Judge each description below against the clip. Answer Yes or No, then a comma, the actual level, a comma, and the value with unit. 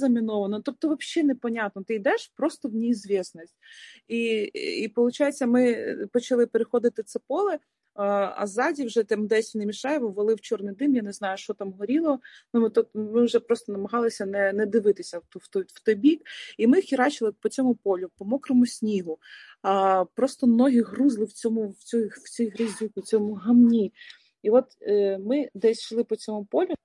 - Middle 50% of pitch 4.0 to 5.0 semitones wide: No, average, 3.6 semitones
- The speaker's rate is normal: No, fast, 185 wpm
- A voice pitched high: Yes, high, 230 Hz